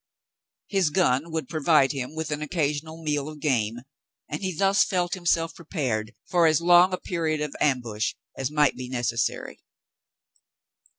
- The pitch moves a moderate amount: Yes, average, 4.1 semitones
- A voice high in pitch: No, medium, 150 Hz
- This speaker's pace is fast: No, average, 155 wpm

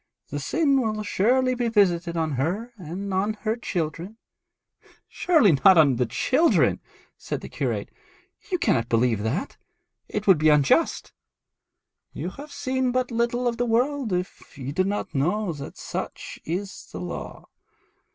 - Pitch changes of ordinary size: No, wide, 7.4 semitones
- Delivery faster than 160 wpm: No, average, 150 wpm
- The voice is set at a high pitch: Yes, high, 200 Hz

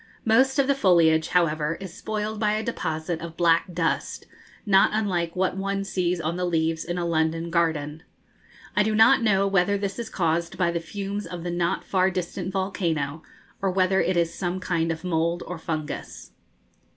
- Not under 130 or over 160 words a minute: No, average, 185 wpm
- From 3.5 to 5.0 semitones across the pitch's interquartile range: No, average, 3.0 semitones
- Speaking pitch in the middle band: Yes, medium, 175 Hz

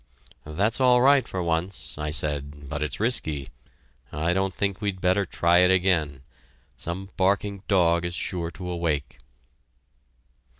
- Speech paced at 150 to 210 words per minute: No, average, 140 wpm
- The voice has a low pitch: Yes, very low, 90 Hz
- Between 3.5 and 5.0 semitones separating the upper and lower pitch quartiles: Yes, average, 3.9 semitones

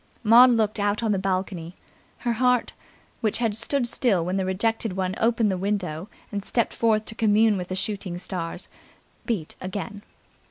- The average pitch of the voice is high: Yes, high, 205 Hz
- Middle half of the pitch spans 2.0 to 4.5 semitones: Yes, average, 3.3 semitones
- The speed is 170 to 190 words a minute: Yes, average, 175 wpm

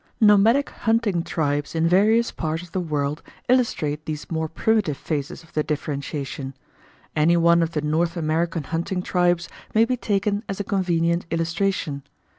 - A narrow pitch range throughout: No, average, 4.3 semitones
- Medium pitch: Yes, medium, 170 Hz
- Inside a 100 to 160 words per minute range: Yes, average, 155 wpm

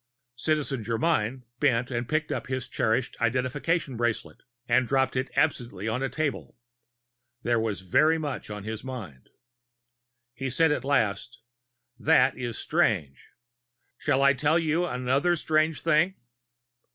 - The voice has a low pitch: Yes, low, 130 Hz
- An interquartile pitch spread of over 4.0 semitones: Yes, average, 4.5 semitones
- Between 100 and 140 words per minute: Yes, slow, 135 wpm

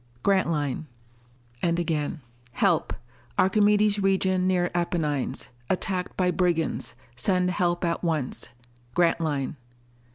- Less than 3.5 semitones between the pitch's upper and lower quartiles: Yes, narrow, 2.6 semitones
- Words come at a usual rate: No, slow, 95 wpm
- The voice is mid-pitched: Yes, medium, 175 Hz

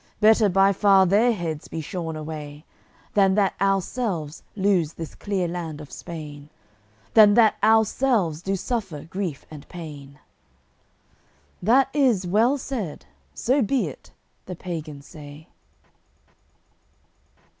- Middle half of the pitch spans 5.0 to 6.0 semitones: Yes, average, 5.3 semitones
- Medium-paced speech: No, slow, 120 wpm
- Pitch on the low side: No, medium, 185 Hz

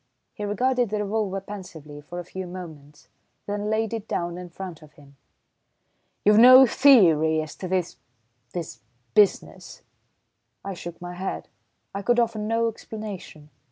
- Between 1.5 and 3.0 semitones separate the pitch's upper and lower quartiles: No, average, 4.2 semitones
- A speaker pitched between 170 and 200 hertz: Yes, high, 190 Hz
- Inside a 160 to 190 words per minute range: No, average, 150 wpm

